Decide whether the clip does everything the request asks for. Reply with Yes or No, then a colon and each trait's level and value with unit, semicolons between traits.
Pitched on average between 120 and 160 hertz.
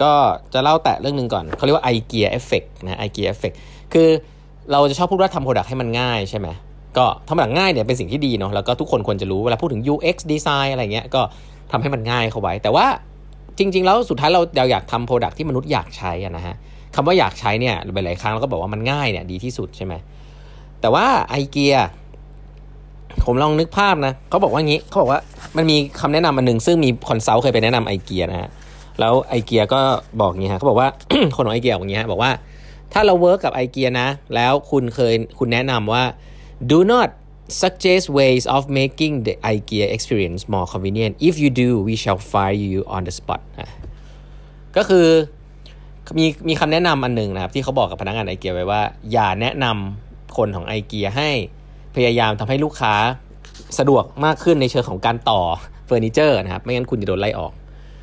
Yes: low, 130 Hz